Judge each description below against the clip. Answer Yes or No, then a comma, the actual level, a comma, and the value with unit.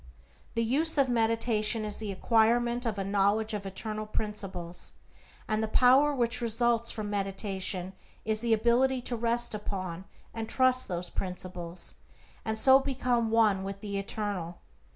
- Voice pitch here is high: Yes, high, 220 Hz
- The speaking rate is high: No, average, 150 wpm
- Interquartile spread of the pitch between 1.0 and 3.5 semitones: Yes, average, 3.2 semitones